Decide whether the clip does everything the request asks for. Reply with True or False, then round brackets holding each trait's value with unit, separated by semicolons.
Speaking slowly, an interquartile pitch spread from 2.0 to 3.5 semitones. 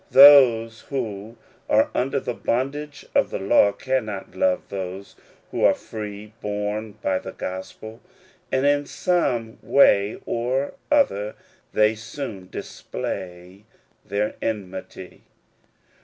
False (110 wpm; 4.6 semitones)